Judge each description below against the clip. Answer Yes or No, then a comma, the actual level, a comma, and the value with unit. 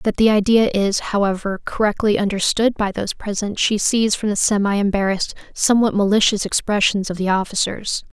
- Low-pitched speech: No, high, 205 Hz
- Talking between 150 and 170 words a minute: Yes, average, 160 wpm